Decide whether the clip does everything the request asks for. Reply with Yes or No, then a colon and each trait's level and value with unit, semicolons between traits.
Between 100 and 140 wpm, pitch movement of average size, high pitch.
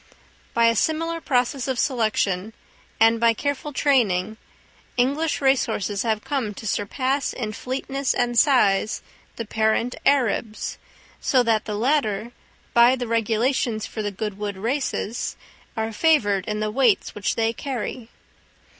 Yes: slow, 135 wpm; average, 3.6 semitones; high, 230 Hz